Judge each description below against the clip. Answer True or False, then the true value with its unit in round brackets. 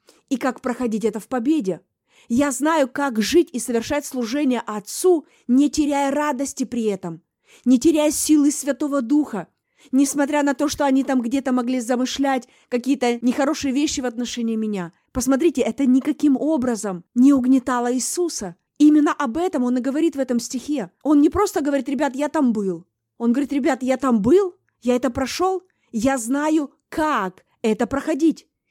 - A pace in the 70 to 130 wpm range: False (160 wpm)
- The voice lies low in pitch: False (270 Hz)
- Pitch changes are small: False (3.3 semitones)